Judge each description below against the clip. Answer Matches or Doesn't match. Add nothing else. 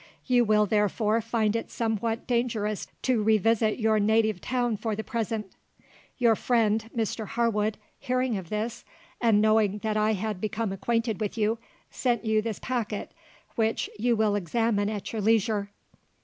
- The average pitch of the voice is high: Matches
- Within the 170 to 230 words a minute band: Doesn't match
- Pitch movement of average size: Doesn't match